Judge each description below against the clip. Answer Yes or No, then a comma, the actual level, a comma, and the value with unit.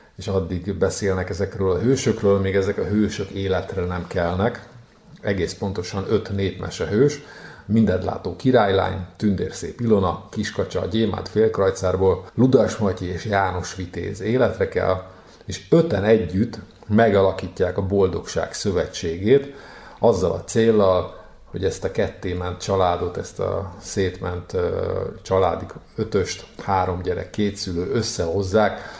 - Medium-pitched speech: No, very low, 95 Hz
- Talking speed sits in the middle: Yes, average, 120 wpm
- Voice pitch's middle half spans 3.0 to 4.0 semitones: No, narrow, 2.4 semitones